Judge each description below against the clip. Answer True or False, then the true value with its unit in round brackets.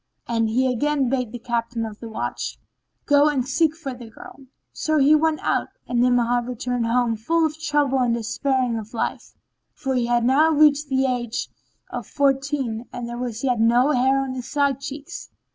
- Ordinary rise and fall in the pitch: True (3.1 semitones)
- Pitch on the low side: False (255 Hz)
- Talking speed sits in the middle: True (190 wpm)